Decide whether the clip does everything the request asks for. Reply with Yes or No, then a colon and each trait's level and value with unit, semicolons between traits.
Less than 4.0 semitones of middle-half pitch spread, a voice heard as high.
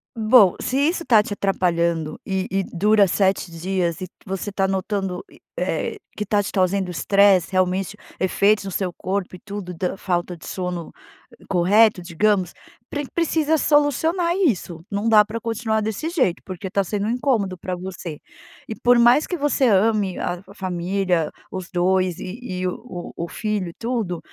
Yes: average, 3.3 semitones; high, 195 Hz